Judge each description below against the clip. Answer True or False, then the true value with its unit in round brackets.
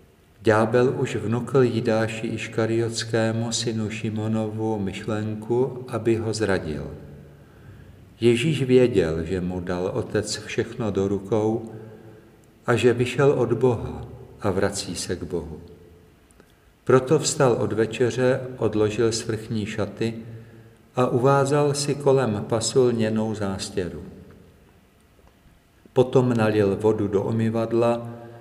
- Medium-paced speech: False (100 wpm)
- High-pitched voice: False (110 Hz)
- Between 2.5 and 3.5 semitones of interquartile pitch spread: True (2.9 semitones)